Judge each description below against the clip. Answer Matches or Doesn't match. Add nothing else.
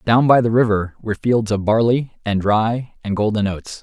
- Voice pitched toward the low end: Matches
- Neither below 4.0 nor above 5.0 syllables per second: Matches